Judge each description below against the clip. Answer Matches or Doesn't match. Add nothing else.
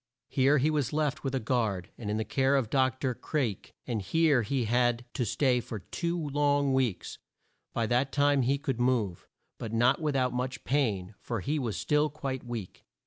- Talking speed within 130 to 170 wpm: Doesn't match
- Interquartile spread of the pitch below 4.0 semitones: Matches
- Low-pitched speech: Matches